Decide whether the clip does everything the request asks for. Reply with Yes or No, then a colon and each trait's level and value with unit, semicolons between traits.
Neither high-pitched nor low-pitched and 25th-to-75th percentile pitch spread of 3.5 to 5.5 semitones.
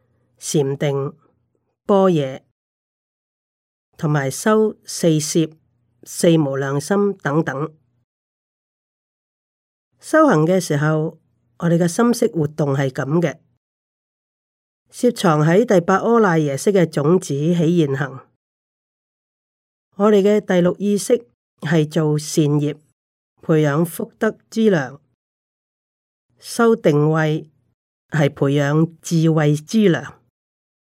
Yes: medium, 160 Hz; average, 4.7 semitones